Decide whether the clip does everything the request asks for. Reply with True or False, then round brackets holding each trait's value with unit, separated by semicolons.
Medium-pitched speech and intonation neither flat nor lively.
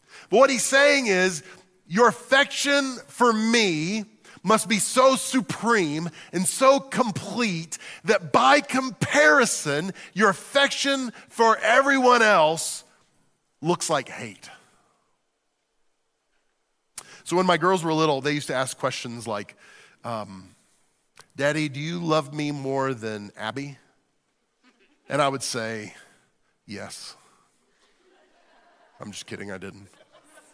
False (175 Hz; 8.9 semitones)